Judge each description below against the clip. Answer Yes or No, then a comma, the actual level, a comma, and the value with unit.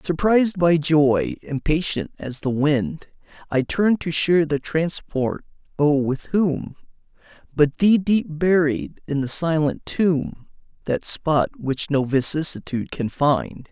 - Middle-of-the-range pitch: Yes, medium, 155 Hz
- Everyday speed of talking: No, slow, 125 wpm